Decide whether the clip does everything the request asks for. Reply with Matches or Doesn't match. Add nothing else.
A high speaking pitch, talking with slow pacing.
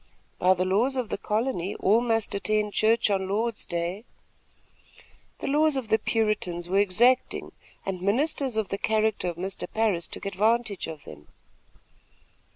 Doesn't match